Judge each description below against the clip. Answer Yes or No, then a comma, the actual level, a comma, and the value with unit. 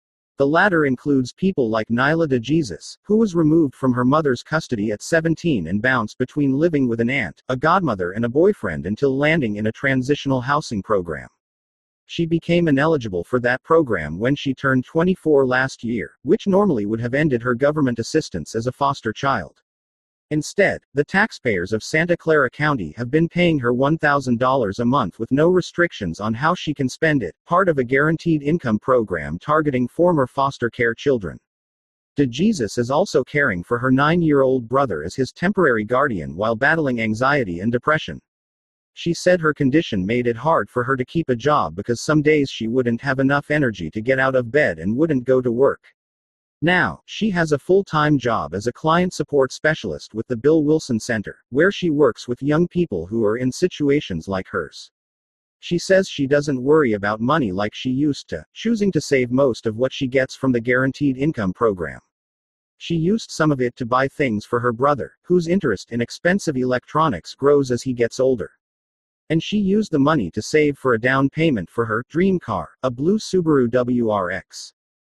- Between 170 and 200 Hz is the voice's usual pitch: No, low, 135 Hz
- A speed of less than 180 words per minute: No, average, 190 wpm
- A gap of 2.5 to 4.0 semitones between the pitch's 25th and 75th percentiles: No, average, 5.0 semitones